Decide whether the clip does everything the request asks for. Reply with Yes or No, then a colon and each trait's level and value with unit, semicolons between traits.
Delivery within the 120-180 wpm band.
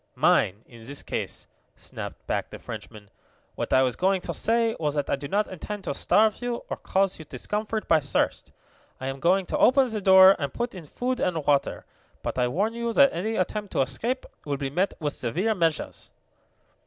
No: fast, 205 wpm